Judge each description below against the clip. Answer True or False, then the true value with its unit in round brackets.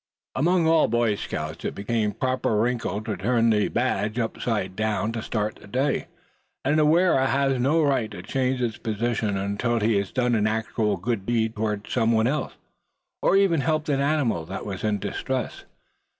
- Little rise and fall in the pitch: False (4.0 semitones)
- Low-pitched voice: True (115 Hz)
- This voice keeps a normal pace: True (190 wpm)